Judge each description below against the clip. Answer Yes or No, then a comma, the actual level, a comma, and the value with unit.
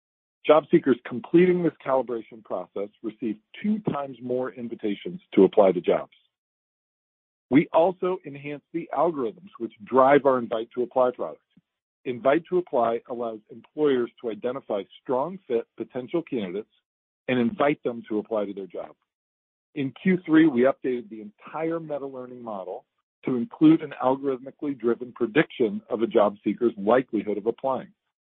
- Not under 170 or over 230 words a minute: No, average, 145 wpm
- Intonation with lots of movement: No, average, 4.8 semitones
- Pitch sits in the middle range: No, low, 130 Hz